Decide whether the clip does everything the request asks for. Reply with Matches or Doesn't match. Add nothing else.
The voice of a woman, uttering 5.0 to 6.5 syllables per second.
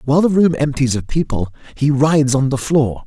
Doesn't match